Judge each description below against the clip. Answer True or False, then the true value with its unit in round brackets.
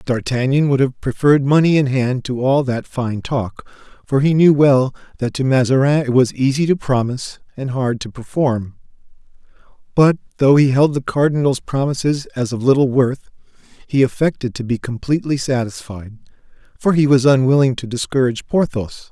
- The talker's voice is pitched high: False (130 Hz)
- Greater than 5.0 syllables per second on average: True (5.2 syllables/s)